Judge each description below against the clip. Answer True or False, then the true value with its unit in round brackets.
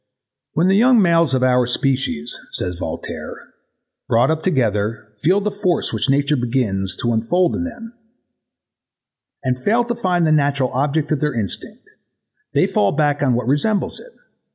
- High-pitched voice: False (145 Hz)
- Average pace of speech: True (160 wpm)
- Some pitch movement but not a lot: False (6.7 semitones)